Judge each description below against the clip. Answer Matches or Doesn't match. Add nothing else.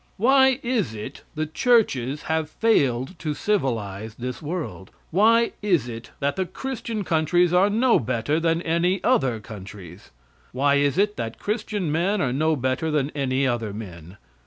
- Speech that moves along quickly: Doesn't match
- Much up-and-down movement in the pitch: Matches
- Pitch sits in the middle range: Matches